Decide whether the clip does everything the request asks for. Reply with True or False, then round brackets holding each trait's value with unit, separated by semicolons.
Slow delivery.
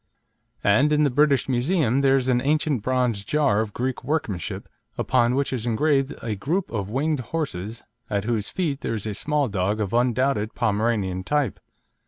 False (175 wpm)